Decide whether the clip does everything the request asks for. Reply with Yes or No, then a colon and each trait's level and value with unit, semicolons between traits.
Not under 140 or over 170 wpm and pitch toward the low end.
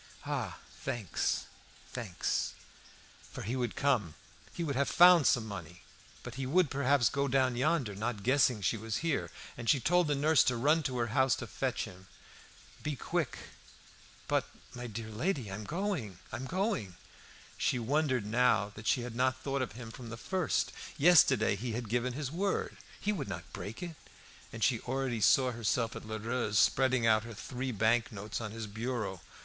No: average, 180 wpm; low, 125 Hz